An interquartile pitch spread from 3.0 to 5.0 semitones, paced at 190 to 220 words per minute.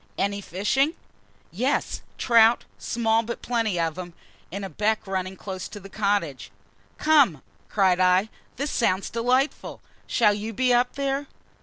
No: average, 4.3 semitones; average, 145 wpm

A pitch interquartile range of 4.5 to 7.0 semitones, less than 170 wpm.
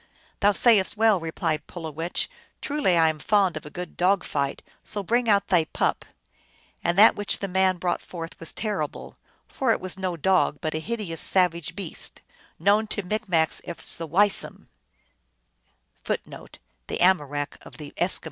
No: average, 3.9 semitones; average, 155 wpm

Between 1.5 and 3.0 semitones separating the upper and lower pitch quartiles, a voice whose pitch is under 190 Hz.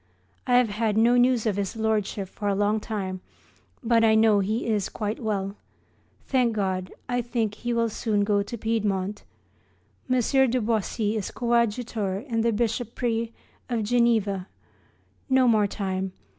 No: narrow, 2.5 semitones; high, 220 Hz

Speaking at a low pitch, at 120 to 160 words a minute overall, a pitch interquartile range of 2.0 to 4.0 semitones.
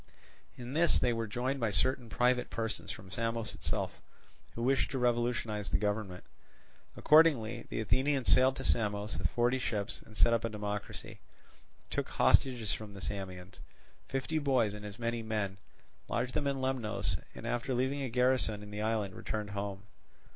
No: low, 115 Hz; average, 170 wpm; average, 3.6 semitones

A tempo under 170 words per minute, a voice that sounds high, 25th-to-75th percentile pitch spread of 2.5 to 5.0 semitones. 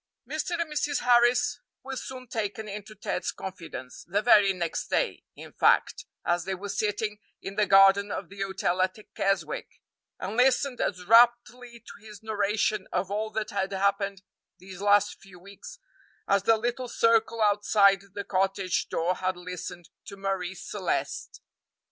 Yes: average, 155 wpm; high, 200 Hz; average, 2.8 semitones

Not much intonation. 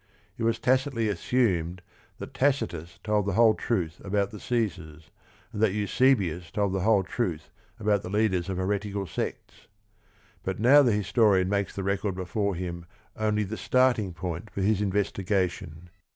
No: average, 3.2 semitones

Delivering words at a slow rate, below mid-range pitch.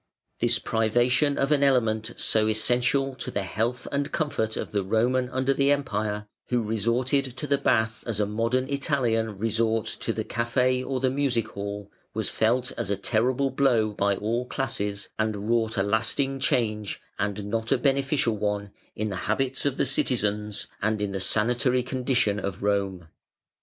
No: average, 170 wpm; low, 115 Hz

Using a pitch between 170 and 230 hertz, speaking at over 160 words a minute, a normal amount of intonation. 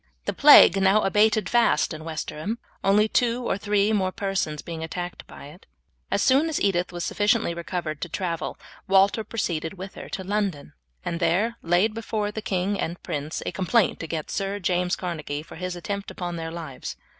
Yes: medium, 185 Hz; average, 180 wpm; average, 3.7 semitones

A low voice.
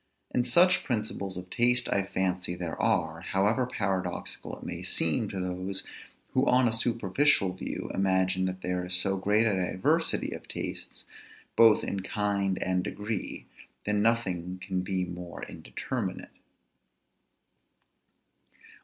Yes: very low, 95 Hz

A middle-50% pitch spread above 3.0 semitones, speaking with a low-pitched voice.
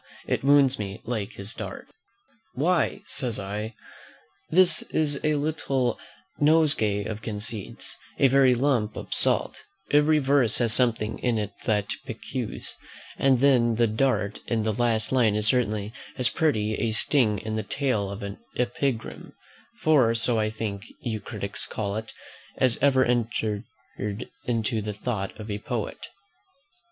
Yes: average, 3.9 semitones; low, 115 Hz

